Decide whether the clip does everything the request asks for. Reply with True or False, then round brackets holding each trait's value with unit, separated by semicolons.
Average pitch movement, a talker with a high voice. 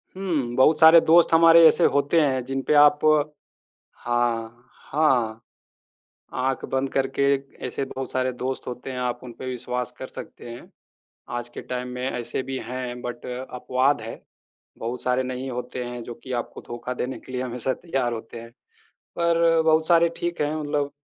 False (3.0 semitones; 130 Hz)